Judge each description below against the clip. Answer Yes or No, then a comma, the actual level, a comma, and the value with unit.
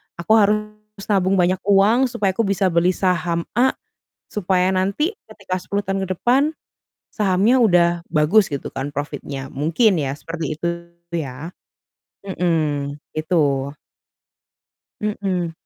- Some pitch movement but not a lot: Yes, average, 4.3 semitones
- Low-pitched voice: No, medium, 185 Hz